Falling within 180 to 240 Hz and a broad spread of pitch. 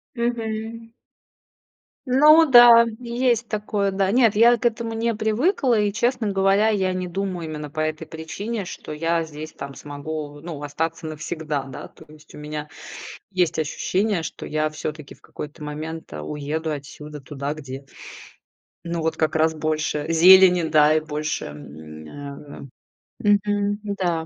No: medium, 165 Hz; wide, 5.7 semitones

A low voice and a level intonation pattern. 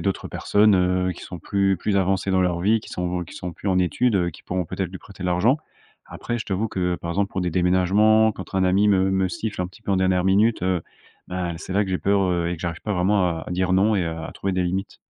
Yes: very low, 95 Hz; narrow, 1.8 semitones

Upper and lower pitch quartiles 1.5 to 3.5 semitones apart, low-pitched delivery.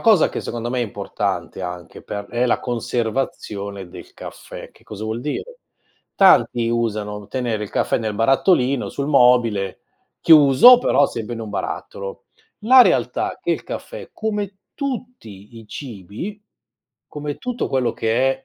No: wide, 5.9 semitones; low, 120 Hz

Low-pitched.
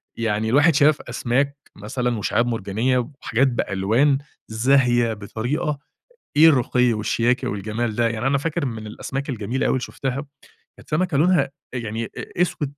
Yes: low, 125 Hz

